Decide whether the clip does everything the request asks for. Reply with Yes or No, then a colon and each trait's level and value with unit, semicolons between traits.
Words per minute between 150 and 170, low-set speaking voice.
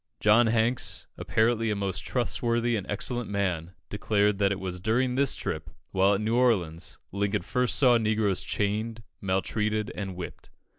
Yes: average, 155 wpm; low, 105 Hz